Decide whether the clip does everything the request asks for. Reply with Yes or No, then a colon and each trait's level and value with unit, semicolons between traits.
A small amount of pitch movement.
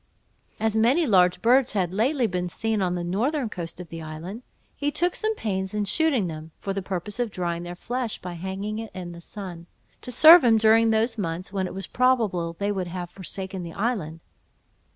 No: average, 4.4 semitones